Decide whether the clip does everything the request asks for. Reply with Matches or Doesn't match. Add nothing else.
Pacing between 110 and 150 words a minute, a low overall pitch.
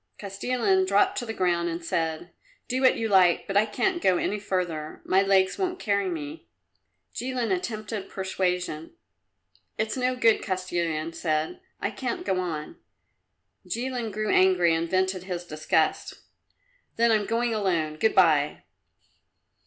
Doesn't match